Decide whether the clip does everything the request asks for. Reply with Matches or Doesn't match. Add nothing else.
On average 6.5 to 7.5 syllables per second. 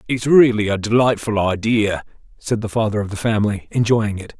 Doesn't match